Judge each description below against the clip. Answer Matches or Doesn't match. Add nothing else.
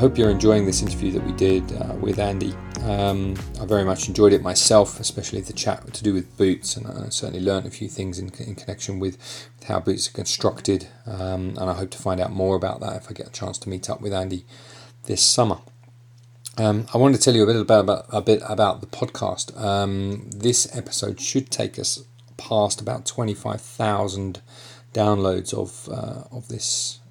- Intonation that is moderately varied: Matches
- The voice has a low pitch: Matches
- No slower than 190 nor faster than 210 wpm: Matches